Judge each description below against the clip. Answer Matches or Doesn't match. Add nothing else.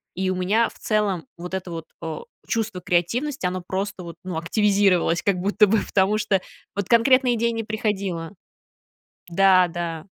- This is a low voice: Doesn't match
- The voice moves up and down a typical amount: Matches